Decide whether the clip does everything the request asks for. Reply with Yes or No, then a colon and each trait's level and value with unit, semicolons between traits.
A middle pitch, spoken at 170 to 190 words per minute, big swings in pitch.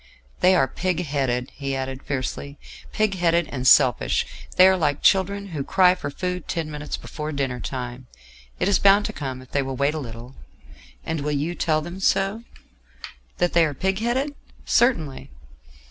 Yes: medium, 155 Hz; average, 175 wpm; wide, 5.7 semitones